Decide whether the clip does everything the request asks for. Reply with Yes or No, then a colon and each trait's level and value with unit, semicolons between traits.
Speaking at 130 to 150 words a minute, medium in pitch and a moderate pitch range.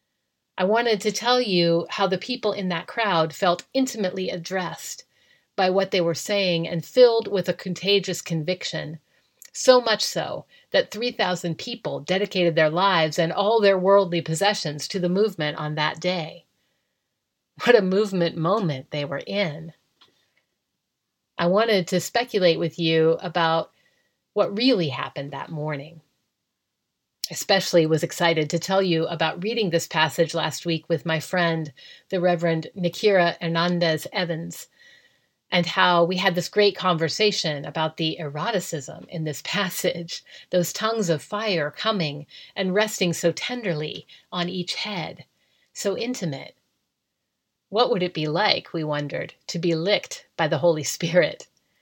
Yes: average, 145 wpm; medium, 175 Hz; average, 3.6 semitones